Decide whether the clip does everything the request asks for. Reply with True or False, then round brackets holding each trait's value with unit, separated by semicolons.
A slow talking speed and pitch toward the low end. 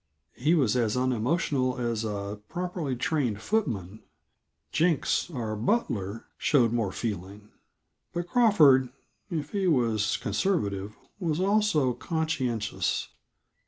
True (105 wpm; 130 Hz)